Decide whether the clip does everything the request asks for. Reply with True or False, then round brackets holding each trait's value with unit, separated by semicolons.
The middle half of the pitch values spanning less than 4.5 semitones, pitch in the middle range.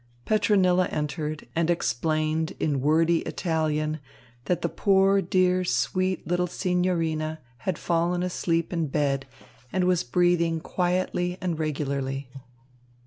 True (2.7 semitones; 165 Hz)